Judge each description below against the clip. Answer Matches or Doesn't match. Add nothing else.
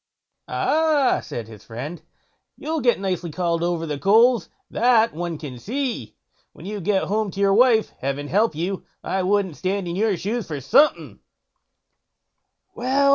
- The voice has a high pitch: Matches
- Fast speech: Doesn't match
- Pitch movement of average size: Doesn't match